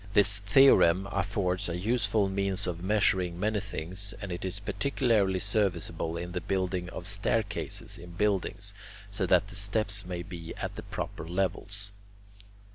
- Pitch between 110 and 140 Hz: No, low, 100 Hz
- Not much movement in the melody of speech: Yes, narrow, 2.3 semitones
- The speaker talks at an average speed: Yes, average, 150 wpm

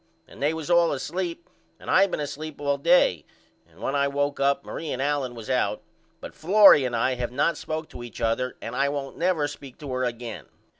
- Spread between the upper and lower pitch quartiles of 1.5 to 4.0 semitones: Yes, average, 3.7 semitones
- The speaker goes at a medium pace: No, fast, 215 wpm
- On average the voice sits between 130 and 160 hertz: Yes, medium, 140 Hz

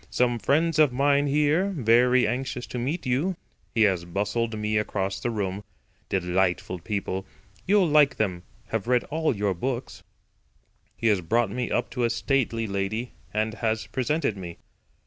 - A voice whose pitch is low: Yes, low, 115 Hz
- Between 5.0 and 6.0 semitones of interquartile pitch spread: Yes, average, 5.3 semitones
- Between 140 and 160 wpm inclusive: Yes, average, 155 wpm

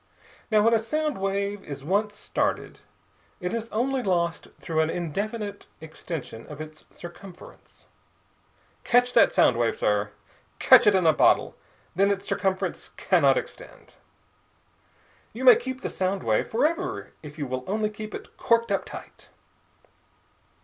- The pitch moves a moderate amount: No, wide, 6.1 semitones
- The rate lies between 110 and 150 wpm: Yes, average, 145 wpm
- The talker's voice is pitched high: Yes, high, 200 Hz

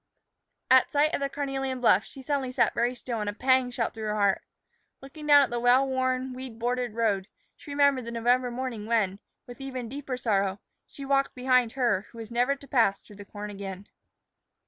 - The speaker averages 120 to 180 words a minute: No, fast, 205 wpm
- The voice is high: Yes, very high, 250 Hz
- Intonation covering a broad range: No, average, 3.2 semitones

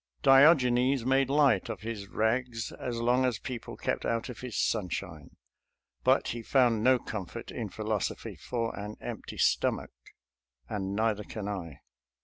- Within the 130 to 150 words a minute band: Yes, average, 145 wpm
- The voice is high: No, low, 115 Hz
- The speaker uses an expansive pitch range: No, average, 3.4 semitones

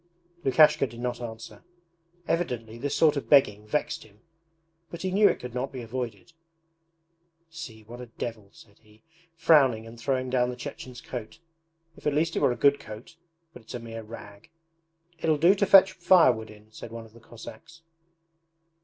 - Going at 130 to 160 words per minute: No, average, 180 wpm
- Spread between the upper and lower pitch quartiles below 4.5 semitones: No, average, 5.1 semitones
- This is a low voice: Yes, low, 125 Hz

